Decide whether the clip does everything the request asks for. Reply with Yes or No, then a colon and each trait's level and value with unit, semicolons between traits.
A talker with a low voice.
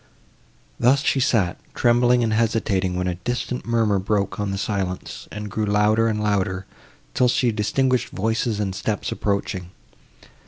Yes: low, 105 Hz